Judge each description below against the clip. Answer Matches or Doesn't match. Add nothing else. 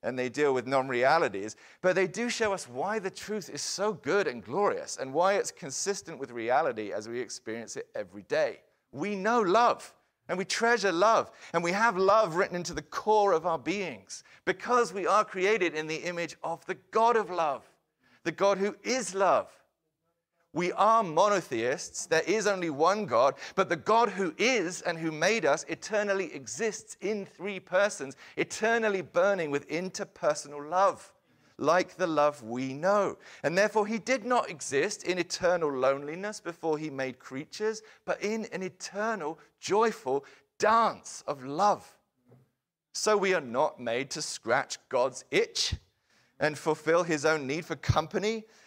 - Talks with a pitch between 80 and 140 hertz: Doesn't match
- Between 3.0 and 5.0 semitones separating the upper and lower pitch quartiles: Doesn't match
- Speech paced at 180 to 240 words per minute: Doesn't match